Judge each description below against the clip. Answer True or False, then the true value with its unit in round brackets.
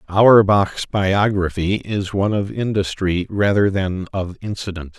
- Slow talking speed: True (120 wpm)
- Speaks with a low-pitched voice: True (100 Hz)